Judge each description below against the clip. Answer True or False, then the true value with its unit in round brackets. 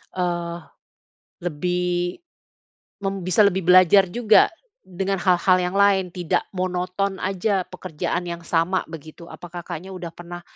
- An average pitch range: False (1.6 semitones)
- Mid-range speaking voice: True (180 Hz)